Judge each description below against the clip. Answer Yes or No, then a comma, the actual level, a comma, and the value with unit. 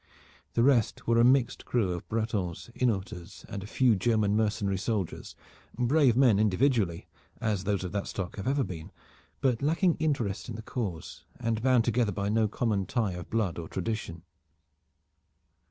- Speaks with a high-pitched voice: No, low, 110 Hz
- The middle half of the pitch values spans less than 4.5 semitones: Yes, average, 3.7 semitones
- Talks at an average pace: Yes, average, 165 wpm